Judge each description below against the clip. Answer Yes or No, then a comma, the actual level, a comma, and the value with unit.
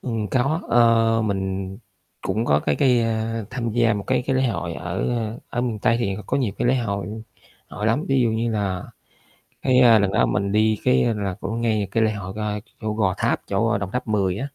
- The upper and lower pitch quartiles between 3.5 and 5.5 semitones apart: No, average, 2.9 semitones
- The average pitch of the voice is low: Yes, low, 110 Hz